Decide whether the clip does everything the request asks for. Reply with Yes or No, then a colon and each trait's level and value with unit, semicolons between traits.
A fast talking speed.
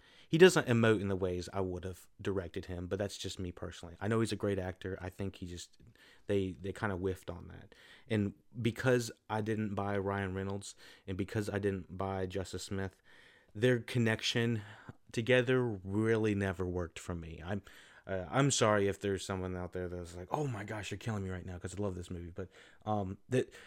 Yes: fast, 210 wpm